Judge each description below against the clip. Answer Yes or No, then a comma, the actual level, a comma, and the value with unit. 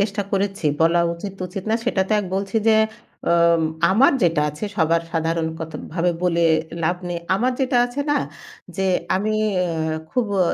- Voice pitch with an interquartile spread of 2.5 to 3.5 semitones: No, average, 4.0 semitones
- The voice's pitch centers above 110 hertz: Yes, medium, 185 Hz